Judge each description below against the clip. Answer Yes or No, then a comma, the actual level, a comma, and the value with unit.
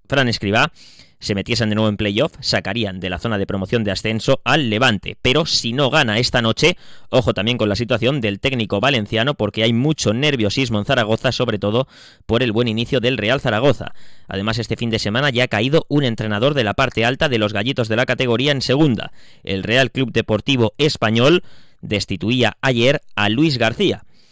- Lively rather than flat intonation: No, average, 3.8 semitones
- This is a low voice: Yes, low, 115 Hz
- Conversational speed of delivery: No, fast, 195 wpm